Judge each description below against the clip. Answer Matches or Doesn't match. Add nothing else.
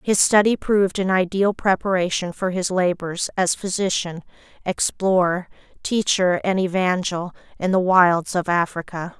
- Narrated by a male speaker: Doesn't match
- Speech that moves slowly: Matches